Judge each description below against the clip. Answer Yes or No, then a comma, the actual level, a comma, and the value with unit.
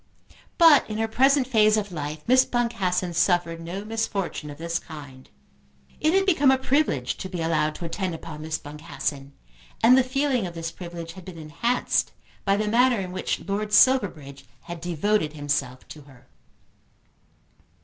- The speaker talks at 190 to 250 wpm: No, average, 165 wpm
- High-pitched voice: No, medium, 180 Hz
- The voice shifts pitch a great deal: Yes, wide, 6.5 semitones